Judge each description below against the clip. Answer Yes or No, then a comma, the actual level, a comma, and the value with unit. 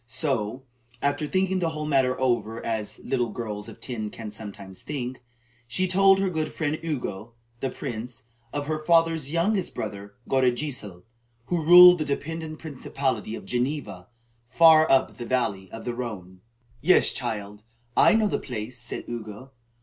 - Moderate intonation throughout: No, wide, 6.0 semitones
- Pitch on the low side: Yes, low, 130 Hz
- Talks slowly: No, average, 155 wpm